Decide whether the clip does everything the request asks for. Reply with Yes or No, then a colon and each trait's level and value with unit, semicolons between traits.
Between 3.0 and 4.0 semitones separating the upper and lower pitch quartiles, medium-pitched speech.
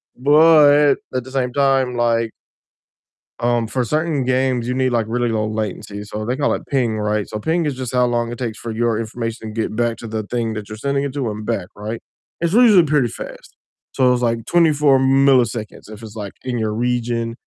No: average, 3.3 semitones; low, 120 Hz